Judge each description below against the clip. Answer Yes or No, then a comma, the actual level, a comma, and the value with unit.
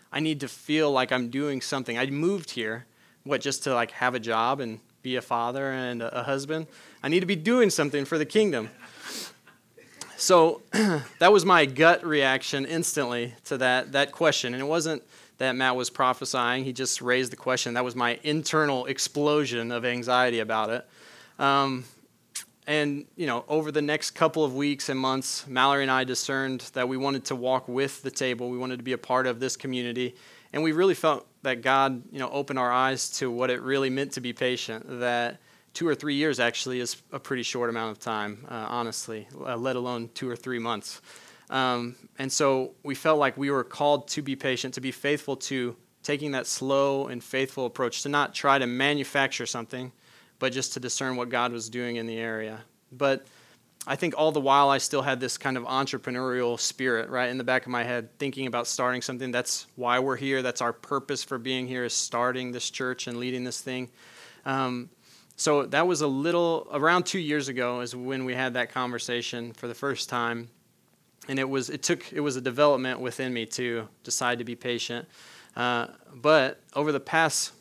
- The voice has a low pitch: Yes, low, 130 Hz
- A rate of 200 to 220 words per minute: Yes, fast, 205 wpm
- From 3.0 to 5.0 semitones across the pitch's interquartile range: No, narrow, 2.5 semitones